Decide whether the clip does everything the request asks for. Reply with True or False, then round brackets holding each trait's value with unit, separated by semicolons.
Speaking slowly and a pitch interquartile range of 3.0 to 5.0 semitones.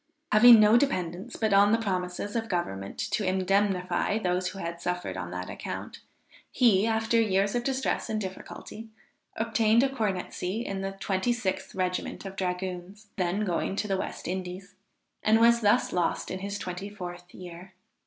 False (165 wpm; 3.3 semitones)